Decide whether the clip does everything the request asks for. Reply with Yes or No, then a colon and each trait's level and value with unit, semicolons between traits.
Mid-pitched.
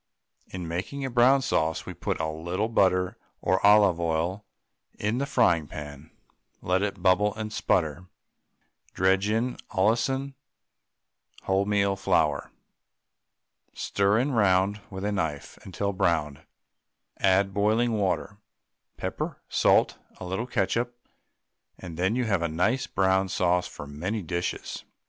No: very low, 95 Hz